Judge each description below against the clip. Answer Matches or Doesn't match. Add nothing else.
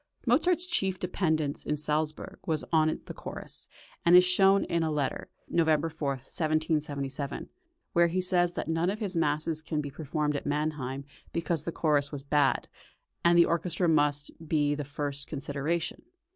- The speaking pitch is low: Doesn't match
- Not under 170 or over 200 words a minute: Doesn't match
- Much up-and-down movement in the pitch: Doesn't match